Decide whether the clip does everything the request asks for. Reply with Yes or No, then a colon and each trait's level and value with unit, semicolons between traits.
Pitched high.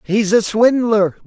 Yes: high, 215 Hz